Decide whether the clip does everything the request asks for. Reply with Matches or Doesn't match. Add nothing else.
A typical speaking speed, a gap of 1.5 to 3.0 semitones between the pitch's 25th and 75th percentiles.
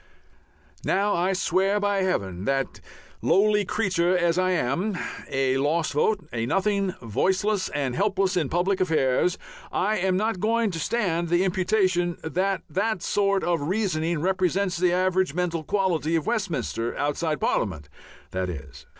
Doesn't match